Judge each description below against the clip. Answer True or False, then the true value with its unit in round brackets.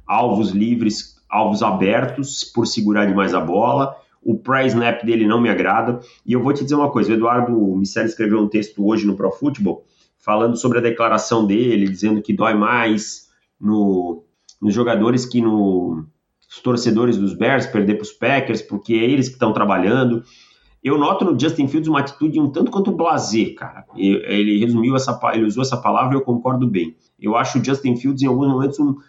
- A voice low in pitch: True (115 Hz)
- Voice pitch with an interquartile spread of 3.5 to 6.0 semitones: True (3.8 semitones)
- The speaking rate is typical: False (190 wpm)